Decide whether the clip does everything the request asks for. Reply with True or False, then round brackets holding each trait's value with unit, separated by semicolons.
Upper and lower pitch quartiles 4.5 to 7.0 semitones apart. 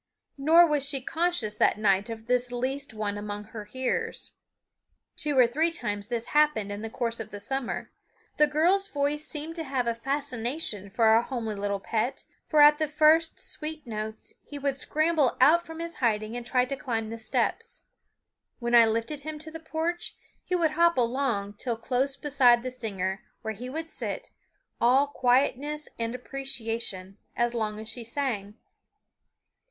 True (5.1 semitones)